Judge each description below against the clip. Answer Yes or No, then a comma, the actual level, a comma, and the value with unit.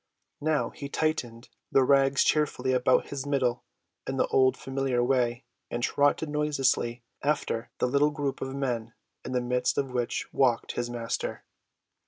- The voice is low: Yes, low, 130 Hz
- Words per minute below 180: Yes, average, 155 wpm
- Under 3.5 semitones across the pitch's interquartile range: Yes, narrow, 2.5 semitones